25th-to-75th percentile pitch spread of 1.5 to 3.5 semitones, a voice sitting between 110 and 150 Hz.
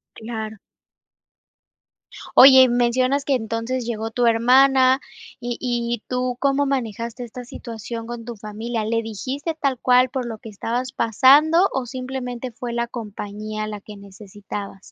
No: narrow, 2.6 semitones; high, 240 Hz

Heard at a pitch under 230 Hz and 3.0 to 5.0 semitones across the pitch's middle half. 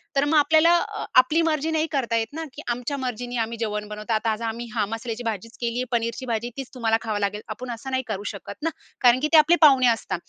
No: high, 240 Hz; average, 3.6 semitones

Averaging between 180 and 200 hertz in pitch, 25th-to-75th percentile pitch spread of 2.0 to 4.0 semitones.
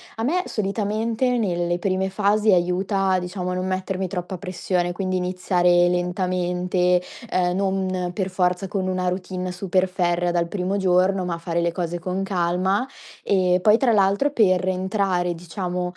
No: medium, 185 Hz; narrow, 1.5 semitones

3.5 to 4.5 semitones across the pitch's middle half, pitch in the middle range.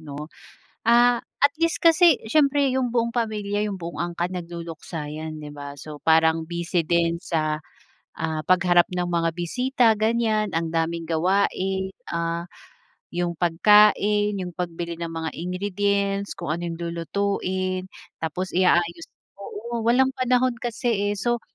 Yes: average, 4.2 semitones; medium, 180 Hz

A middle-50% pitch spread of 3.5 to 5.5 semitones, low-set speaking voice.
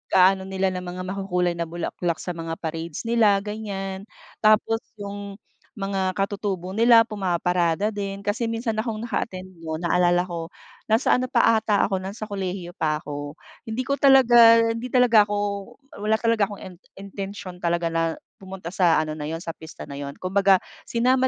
No: average, 3.8 semitones; high, 195 Hz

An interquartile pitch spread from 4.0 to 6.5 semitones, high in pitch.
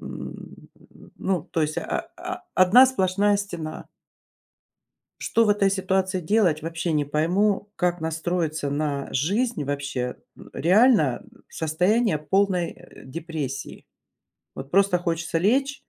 No: average, 4.6 semitones; medium, 180 Hz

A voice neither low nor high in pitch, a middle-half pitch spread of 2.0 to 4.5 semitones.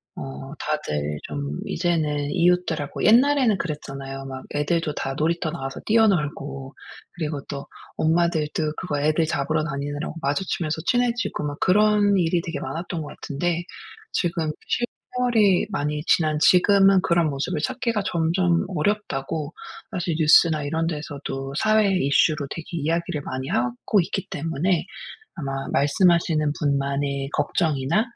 Yes: medium, 160 Hz; average, 3.8 semitones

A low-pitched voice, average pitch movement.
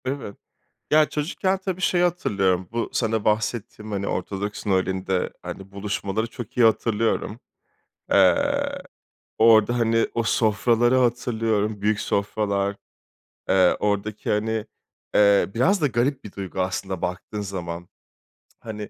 Yes: low, 105 Hz; average, 3.0 semitones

